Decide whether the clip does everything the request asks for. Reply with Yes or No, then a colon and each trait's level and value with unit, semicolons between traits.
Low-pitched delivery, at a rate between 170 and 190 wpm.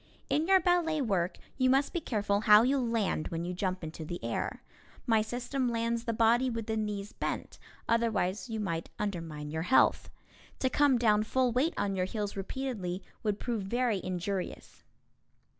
No: high, 220 Hz; average, 175 wpm